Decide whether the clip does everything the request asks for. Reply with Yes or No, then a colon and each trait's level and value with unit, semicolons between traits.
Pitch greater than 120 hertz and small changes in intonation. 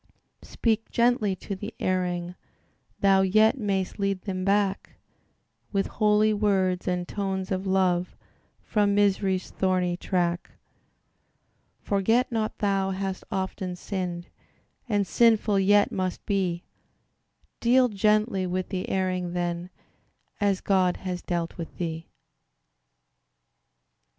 Yes: high, 190 Hz; narrow, 2.1 semitones